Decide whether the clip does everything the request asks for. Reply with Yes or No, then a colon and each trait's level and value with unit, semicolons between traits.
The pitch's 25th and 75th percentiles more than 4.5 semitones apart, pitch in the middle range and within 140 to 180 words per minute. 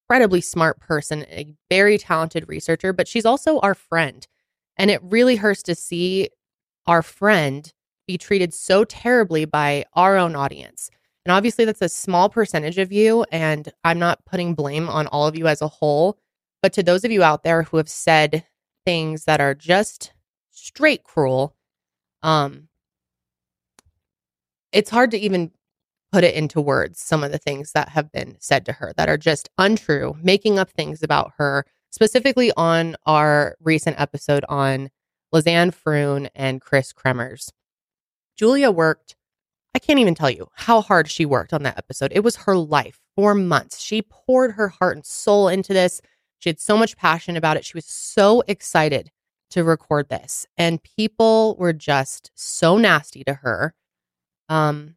Yes: average, 5.1 semitones; medium, 165 Hz; average, 170 wpm